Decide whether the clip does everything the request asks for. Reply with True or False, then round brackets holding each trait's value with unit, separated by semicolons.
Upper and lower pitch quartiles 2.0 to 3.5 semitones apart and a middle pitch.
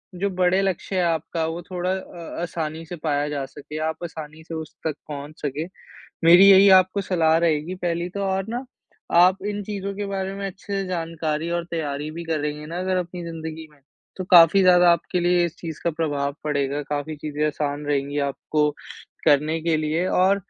True (3.2 semitones; 165 Hz)